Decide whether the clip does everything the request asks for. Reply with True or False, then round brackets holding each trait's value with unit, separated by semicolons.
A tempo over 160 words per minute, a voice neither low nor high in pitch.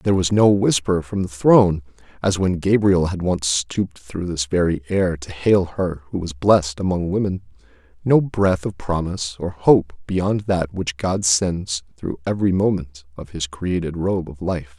False (185 wpm; 90 Hz)